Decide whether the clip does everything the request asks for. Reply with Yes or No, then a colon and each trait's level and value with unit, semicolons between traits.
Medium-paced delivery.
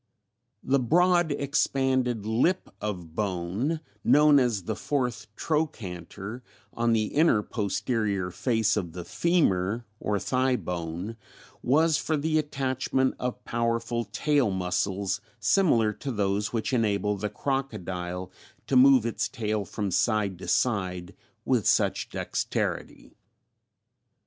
No: slow, 120 wpm